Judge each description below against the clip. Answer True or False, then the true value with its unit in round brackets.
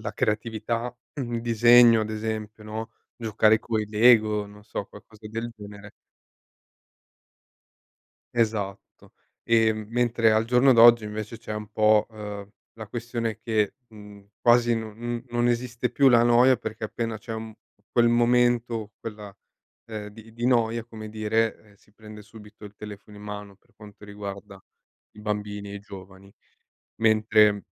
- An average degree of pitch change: False (1.9 semitones)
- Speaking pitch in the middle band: False (110 Hz)